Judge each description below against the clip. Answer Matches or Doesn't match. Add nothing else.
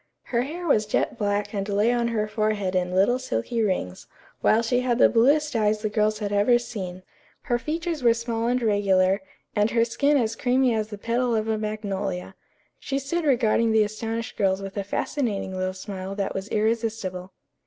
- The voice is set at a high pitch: Matches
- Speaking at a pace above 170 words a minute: Matches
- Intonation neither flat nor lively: Matches